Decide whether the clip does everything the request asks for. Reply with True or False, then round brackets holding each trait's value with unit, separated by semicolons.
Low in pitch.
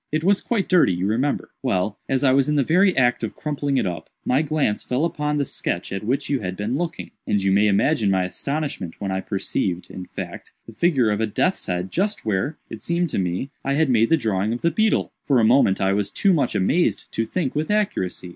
True (125 Hz)